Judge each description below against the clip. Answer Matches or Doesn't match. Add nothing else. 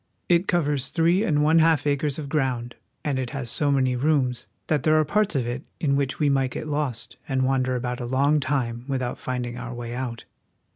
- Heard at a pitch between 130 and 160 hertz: Matches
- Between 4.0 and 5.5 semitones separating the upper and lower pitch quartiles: Doesn't match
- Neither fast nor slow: Doesn't match